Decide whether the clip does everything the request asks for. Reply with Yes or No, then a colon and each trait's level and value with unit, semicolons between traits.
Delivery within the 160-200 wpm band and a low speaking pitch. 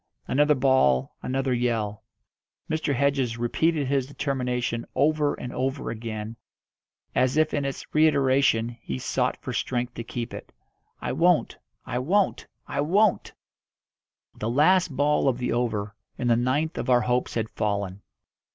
No: average, 145 wpm; low, 130 Hz